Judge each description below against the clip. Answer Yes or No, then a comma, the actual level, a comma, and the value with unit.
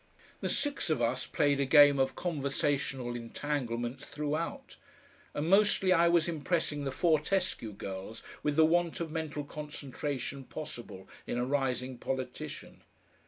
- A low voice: No, medium, 145 Hz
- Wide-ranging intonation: No, average, 3.7 semitones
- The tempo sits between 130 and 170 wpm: Yes, slow, 135 wpm